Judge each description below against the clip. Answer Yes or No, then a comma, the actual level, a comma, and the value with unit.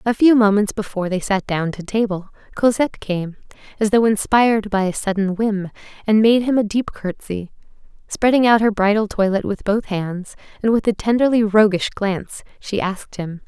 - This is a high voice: Yes, high, 210 Hz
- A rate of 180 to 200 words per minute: Yes, average, 185 wpm